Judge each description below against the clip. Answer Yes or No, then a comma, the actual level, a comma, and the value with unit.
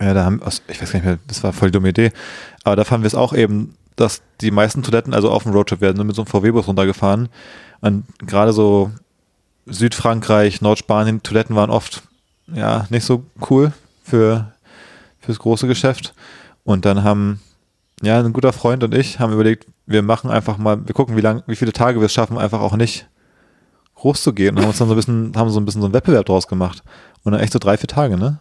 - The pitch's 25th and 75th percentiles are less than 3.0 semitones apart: Yes, narrow, 2.4 semitones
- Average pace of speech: No, fast, 225 wpm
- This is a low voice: Yes, low, 110 Hz